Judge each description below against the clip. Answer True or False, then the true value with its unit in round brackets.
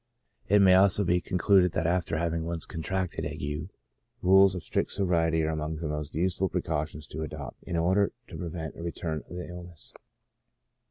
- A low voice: True (85 Hz)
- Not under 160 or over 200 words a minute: True (180 wpm)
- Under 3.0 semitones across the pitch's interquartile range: True (2.5 semitones)